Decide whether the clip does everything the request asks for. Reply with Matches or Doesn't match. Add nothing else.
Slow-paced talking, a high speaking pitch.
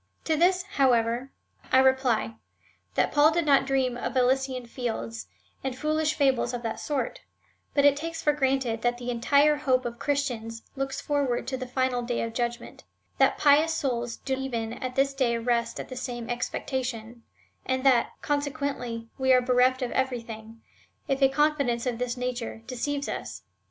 Doesn't match